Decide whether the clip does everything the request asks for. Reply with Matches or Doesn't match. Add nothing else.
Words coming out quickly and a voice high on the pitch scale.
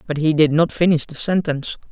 Doesn't match